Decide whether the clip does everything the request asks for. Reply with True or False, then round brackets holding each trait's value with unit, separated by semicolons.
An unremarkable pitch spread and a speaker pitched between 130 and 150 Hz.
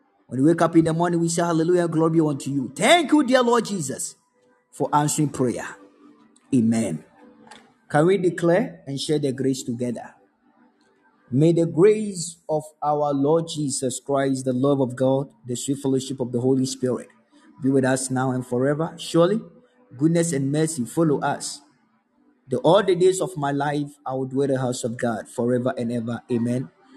True (4.4 semitones; 140 Hz)